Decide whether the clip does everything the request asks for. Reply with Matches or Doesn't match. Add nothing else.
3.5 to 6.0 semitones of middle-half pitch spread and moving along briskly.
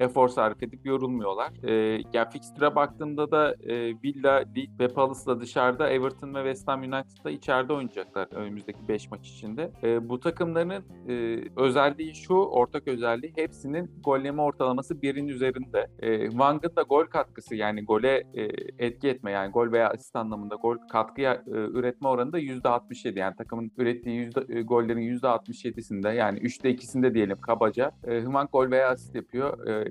Doesn't match